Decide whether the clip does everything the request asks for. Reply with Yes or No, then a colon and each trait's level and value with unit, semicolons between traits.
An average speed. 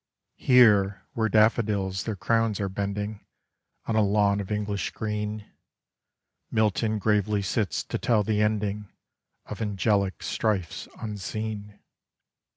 No: slow, 115 wpm